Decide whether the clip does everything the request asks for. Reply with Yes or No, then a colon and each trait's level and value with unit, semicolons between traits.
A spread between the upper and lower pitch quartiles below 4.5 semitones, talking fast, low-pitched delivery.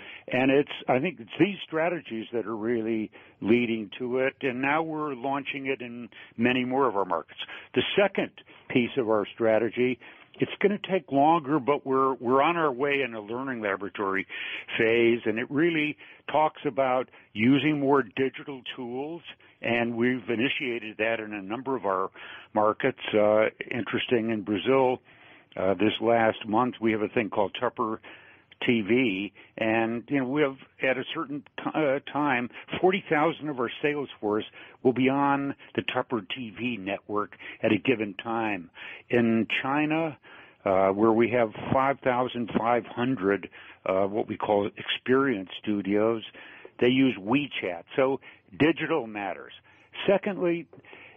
No: average, 3.8 semitones; average, 150 wpm; low, 125 Hz